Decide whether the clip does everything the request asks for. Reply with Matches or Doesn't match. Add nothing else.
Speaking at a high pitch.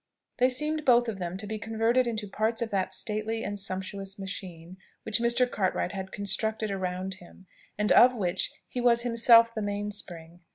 Matches